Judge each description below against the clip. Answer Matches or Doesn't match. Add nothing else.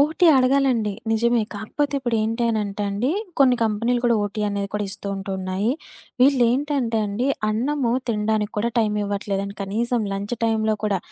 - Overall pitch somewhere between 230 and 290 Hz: Doesn't match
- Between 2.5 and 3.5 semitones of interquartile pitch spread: Matches